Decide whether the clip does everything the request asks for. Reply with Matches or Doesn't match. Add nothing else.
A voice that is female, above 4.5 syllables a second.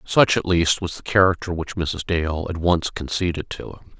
Doesn't match